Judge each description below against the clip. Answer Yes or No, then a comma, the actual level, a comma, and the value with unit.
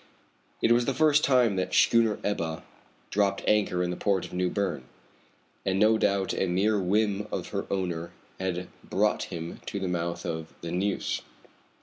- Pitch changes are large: No, average, 3.0 semitones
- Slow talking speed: No, average, 185 wpm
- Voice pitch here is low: Yes, very low, 95 Hz